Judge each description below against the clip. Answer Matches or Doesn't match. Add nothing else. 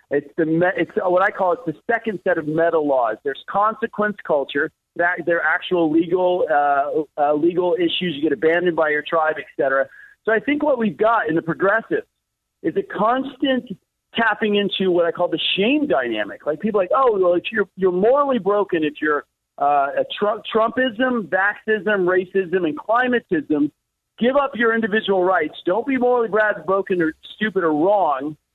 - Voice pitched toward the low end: Doesn't match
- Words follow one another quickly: Doesn't match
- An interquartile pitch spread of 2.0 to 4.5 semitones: Doesn't match